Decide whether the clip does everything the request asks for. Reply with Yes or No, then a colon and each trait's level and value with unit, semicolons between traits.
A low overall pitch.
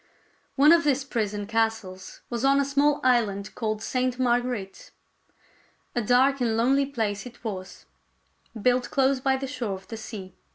No: high, 245 Hz